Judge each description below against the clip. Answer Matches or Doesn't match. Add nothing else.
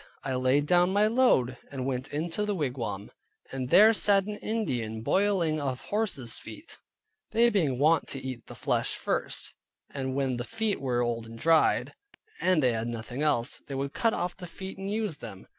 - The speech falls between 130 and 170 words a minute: Doesn't match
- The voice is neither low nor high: Matches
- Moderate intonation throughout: Doesn't match